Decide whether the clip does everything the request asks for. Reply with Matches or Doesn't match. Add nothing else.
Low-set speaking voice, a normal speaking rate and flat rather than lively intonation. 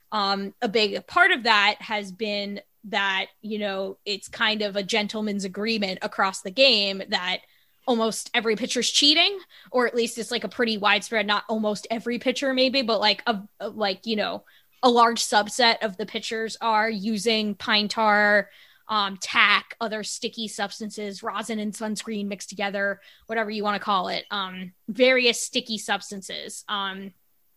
Doesn't match